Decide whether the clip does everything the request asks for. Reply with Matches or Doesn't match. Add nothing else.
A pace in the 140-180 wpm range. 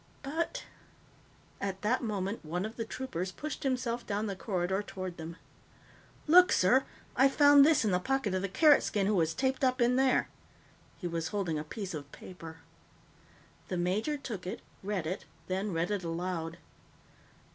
Matches